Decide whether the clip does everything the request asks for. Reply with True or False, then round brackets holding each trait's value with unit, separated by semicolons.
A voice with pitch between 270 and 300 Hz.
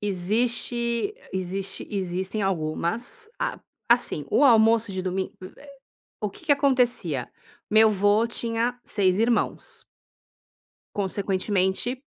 False (210 Hz)